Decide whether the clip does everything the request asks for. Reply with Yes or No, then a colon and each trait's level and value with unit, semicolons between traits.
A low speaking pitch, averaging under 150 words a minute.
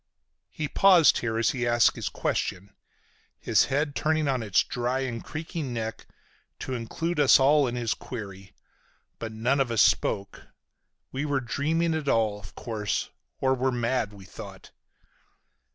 No: low, 125 Hz; average, 155 wpm